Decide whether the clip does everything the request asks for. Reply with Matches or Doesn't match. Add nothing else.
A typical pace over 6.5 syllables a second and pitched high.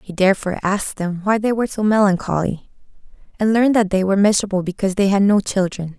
Matches